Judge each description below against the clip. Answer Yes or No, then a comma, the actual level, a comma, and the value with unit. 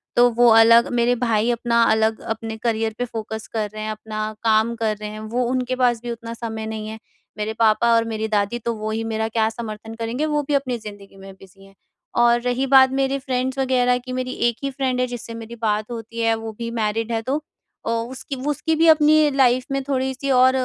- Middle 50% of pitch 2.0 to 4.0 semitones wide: Yes, narrow, 2.4 semitones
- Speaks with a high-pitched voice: Yes, high, 230 Hz